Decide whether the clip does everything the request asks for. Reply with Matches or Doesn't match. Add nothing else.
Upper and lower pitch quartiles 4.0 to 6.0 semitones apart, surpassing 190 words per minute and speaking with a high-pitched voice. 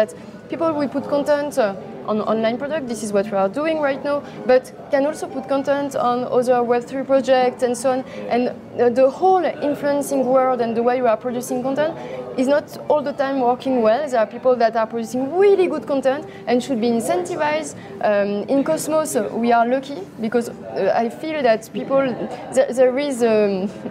Doesn't match